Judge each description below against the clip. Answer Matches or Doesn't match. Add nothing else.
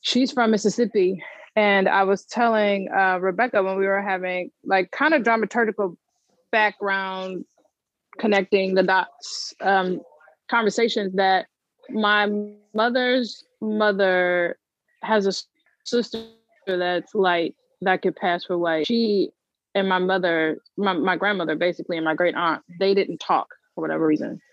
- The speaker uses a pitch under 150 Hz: Doesn't match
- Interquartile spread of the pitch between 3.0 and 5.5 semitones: Matches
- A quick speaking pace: Doesn't match